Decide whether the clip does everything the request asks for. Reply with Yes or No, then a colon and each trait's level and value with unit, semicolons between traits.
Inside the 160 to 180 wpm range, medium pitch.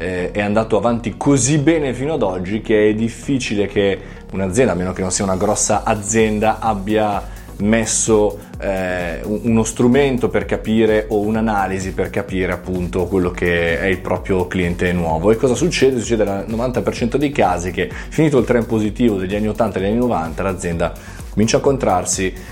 No: fast, 170 wpm; low, 105 Hz